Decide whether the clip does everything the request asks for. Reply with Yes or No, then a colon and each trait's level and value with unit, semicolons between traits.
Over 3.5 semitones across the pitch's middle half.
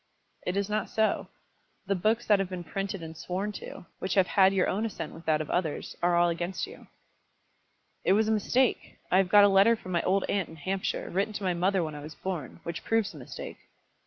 No: average, 2.9 semitones